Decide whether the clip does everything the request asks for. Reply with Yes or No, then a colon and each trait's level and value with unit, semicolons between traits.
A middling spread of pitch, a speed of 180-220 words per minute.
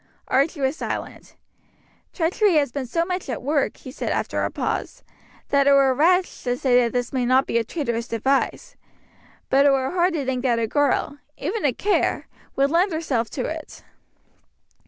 Yes: average, 4.2 semitones; average, 185 wpm